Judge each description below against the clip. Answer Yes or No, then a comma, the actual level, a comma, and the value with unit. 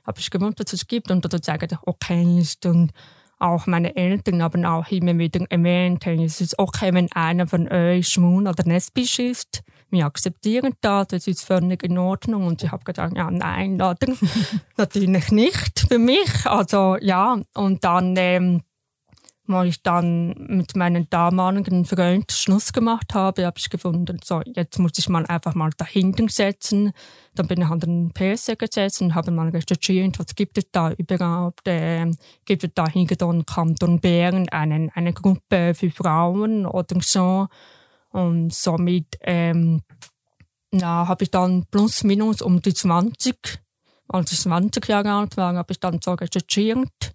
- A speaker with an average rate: Yes, average, 165 wpm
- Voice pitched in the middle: Yes, medium, 180 Hz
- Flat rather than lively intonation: Yes, narrow, 2.2 semitones